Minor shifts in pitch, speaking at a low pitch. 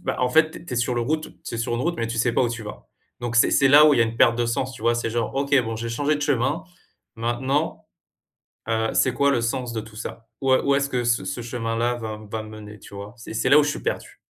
No: average, 3.2 semitones; low, 120 Hz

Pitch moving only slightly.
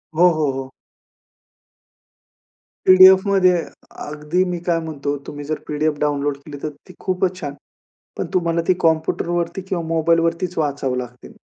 No: average, 3.5 semitones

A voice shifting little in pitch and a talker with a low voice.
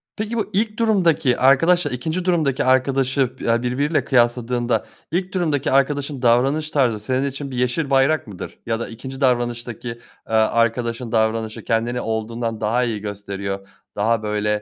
No: average, 3.8 semitones; low, 125 Hz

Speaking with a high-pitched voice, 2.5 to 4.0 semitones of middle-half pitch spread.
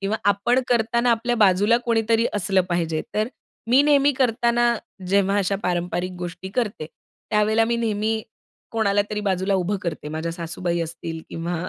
No: high, 205 Hz; average, 4.6 semitones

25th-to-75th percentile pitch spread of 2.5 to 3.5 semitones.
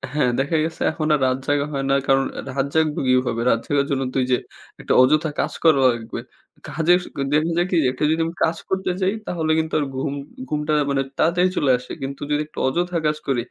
Yes: average, 3.2 semitones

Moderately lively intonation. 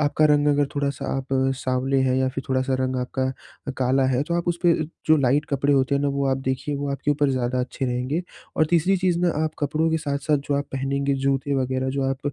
No: narrow, 2.0 semitones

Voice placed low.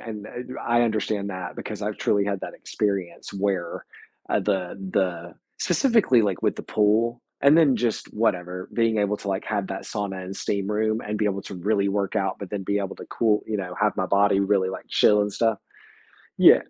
Yes: low, 100 Hz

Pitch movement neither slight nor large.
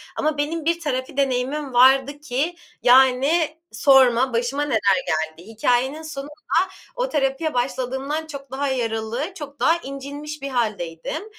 Yes: average, 3.3 semitones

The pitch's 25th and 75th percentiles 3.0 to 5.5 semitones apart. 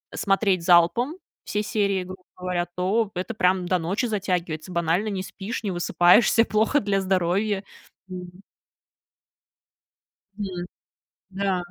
No: narrow, 2.5 semitones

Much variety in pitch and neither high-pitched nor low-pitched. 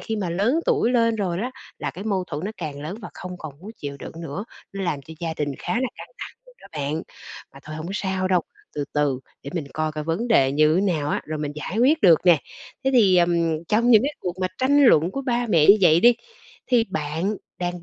Yes: wide, 5.7 semitones; medium, 175 Hz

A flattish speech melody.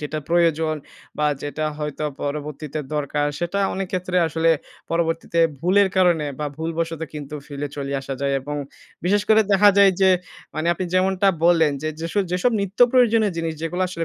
No: average, 3.5 semitones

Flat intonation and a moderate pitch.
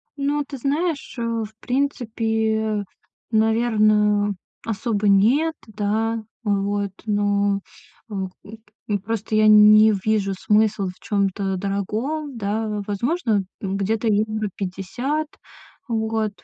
No: narrow, 2.0 semitones; high, 215 Hz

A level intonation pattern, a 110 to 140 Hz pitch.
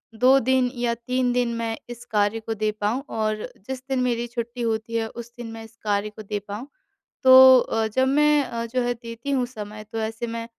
No: narrow, 2.2 semitones; high, 235 Hz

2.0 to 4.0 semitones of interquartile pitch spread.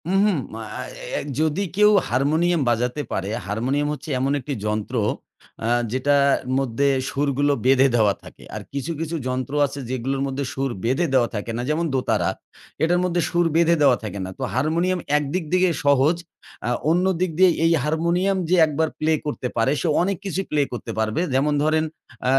No: average, 4.7 semitones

